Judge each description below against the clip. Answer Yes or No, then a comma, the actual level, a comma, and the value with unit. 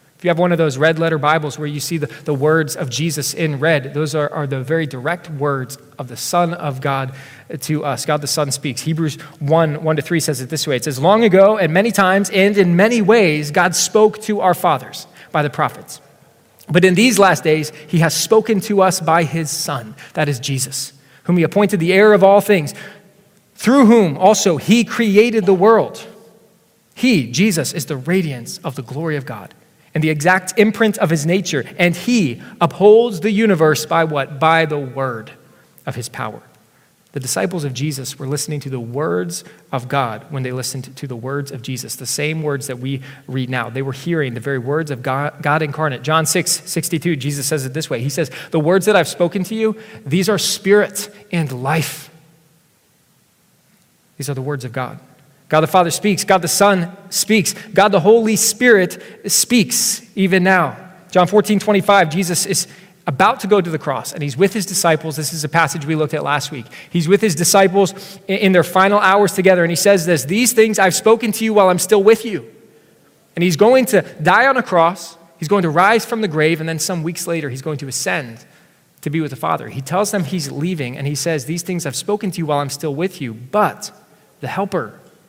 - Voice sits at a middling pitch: Yes, medium, 165 Hz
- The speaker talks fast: Yes, fast, 215 wpm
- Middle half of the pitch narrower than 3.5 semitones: No, average, 5.0 semitones